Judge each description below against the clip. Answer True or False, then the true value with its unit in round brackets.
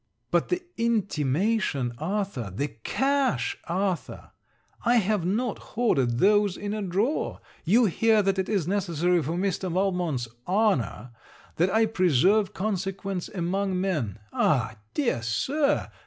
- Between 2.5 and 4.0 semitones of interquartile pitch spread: False (4.6 semitones)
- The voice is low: False (190 Hz)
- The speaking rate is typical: False (125 wpm)